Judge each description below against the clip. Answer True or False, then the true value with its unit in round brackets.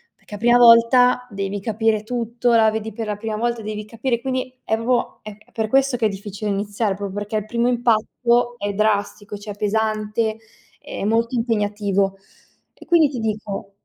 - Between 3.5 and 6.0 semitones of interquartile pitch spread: False (2.4 semitones)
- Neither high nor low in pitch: False (220 Hz)